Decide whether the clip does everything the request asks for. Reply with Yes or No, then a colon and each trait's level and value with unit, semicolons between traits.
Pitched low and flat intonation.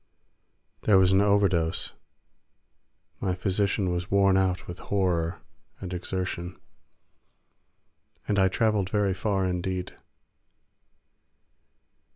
Yes: very low, 95 Hz; narrow, 1.7 semitones